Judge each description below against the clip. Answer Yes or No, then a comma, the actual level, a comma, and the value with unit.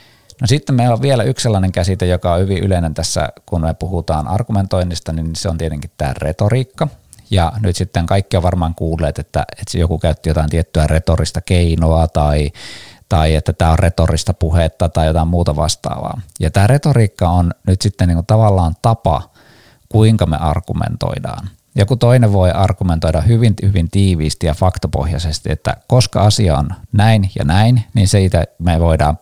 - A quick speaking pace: Yes, fast, 165 wpm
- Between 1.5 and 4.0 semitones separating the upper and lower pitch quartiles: No, average, 4.5 semitones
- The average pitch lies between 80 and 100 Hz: Yes, very low, 90 Hz